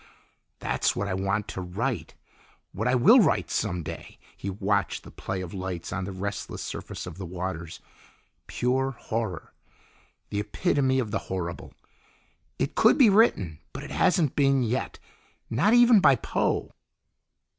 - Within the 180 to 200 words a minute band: No, average, 155 wpm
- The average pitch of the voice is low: Yes, low, 105 Hz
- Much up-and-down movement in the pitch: Yes, wide, 6.1 semitones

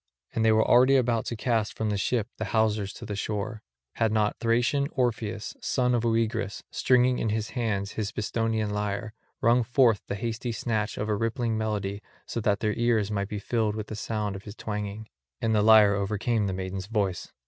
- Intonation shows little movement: Yes, narrow, 2.0 semitones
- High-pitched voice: No, low, 110 Hz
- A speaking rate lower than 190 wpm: No, average, 200 wpm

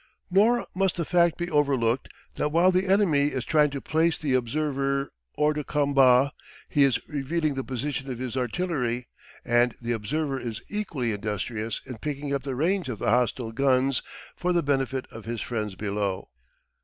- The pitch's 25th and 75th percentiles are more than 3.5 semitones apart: Yes, average, 4.2 semitones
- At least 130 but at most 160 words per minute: No, average, 175 wpm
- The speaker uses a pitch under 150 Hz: Yes, low, 135 Hz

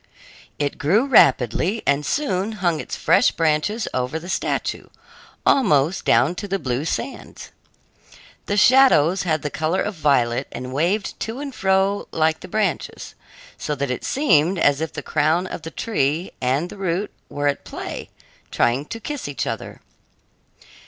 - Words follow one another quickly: No, average, 160 wpm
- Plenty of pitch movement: Yes, wide, 5.8 semitones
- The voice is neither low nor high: Yes, medium, 165 Hz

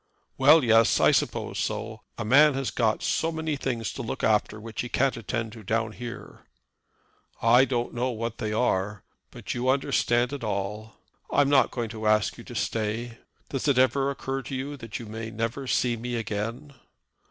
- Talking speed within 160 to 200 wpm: Yes, average, 185 wpm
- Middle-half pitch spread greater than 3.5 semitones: No, average, 3.2 semitones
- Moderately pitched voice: No, low, 120 Hz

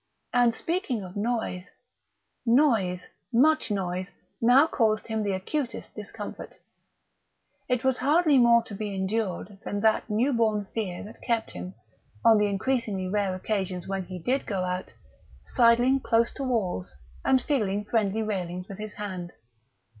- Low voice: No, high, 215 Hz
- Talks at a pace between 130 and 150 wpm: Yes, average, 145 wpm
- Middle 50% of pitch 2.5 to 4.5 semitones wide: Yes, average, 3.9 semitones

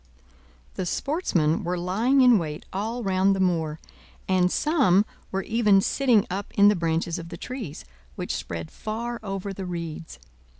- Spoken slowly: No, average, 160 wpm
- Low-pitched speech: No, high, 190 Hz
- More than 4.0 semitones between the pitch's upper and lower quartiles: Yes, average, 4.5 semitones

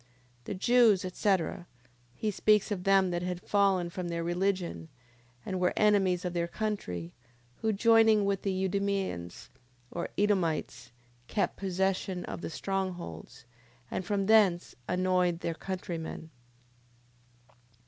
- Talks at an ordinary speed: No, slow, 130 wpm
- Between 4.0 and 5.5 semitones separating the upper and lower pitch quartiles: No, narrow, 2.5 semitones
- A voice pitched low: No, medium, 185 Hz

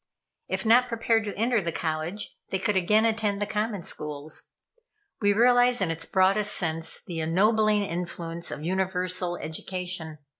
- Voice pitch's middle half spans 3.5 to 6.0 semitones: Yes, average, 4.1 semitones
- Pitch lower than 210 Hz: Yes, high, 190 Hz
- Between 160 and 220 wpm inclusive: No, average, 150 wpm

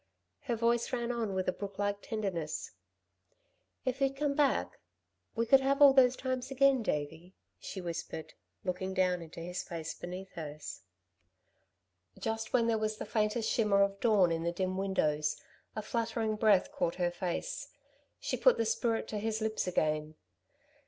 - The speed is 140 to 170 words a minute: Yes, average, 160 wpm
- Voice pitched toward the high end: Yes, high, 210 Hz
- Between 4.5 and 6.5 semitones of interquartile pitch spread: Yes, average, 4.8 semitones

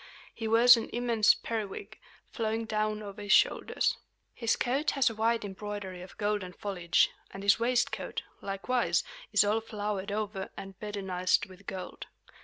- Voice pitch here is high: Yes, high, 210 Hz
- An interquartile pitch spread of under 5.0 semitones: Yes, narrow, 2.6 semitones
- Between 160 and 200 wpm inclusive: No, average, 150 wpm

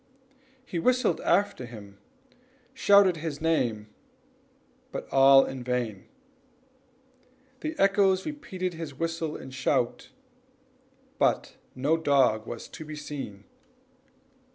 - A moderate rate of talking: No, slow, 105 wpm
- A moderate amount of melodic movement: No, wide, 6.6 semitones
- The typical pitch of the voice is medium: Yes, medium, 150 Hz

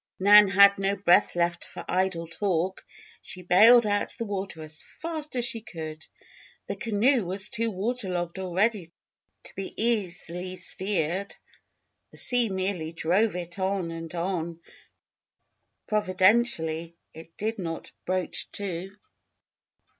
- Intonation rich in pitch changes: No, average, 3.4 semitones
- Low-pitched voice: No, high, 190 Hz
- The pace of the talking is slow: Yes, slow, 130 wpm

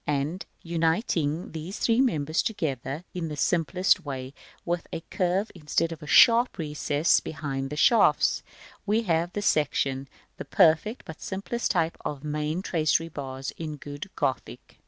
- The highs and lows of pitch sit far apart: No, average, 3.5 semitones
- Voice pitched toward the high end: No, medium, 160 Hz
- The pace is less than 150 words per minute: No, average, 155 wpm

